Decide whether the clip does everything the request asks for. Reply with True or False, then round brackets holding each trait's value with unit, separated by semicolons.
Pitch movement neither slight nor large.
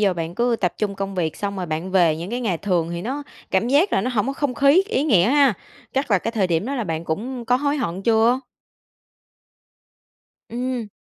False (6.0 semitones)